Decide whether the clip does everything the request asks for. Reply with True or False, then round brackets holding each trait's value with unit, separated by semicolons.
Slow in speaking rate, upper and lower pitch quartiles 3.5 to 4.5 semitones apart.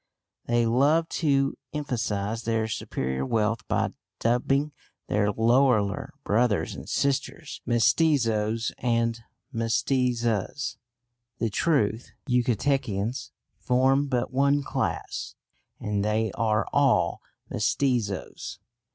True (100 wpm; 3.8 semitones)